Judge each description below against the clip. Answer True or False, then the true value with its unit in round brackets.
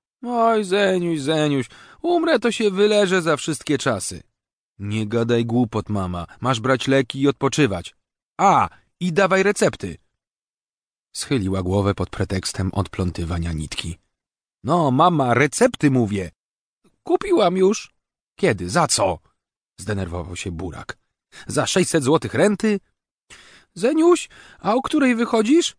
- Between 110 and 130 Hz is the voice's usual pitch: False (140 Hz)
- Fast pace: False (115 wpm)